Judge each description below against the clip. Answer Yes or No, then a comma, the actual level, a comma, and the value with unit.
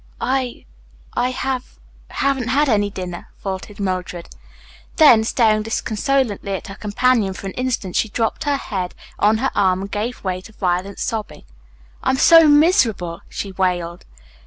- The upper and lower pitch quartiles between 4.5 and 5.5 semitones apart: Yes, average, 5.1 semitones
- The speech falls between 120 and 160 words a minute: Yes, average, 155 wpm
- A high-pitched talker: Yes, high, 215 Hz